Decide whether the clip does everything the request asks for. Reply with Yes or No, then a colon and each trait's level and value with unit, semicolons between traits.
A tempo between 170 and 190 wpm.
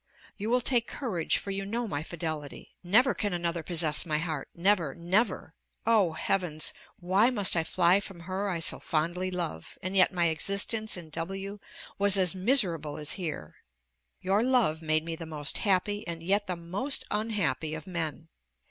Yes: average, 175 wpm